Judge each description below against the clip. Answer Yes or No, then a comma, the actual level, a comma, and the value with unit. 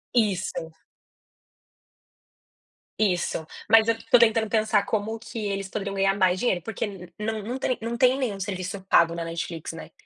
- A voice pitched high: Yes, high, 200 Hz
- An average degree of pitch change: Yes, average, 3.3 semitones